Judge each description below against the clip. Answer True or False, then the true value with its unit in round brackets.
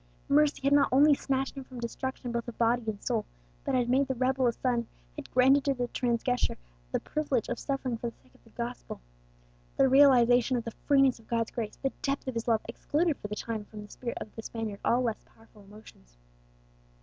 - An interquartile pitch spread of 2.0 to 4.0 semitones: True (2.9 semitones)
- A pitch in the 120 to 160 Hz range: False (245 Hz)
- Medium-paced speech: False (220 wpm)